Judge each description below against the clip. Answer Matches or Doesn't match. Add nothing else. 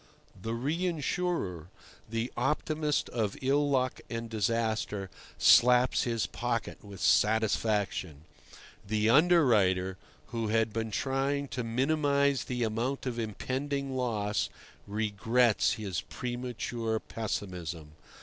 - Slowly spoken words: Matches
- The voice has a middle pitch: Doesn't match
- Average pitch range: Matches